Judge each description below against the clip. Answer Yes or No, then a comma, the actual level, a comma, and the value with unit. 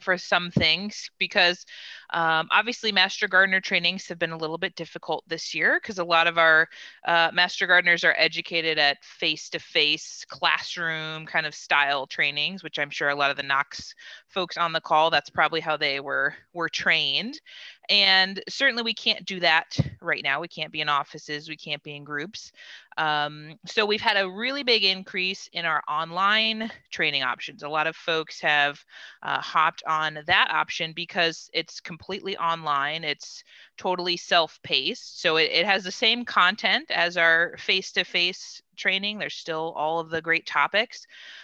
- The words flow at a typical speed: Yes, average, 175 wpm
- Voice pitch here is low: No, medium, 170 Hz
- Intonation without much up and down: No, average, 3.5 semitones